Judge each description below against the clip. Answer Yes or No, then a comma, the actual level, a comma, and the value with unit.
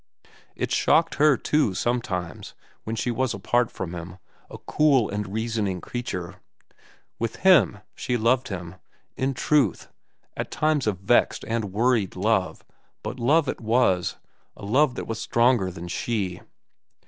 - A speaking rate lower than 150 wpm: Yes, average, 140 wpm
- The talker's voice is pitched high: No, low, 115 Hz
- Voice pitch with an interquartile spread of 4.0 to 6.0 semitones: Yes, average, 5.1 semitones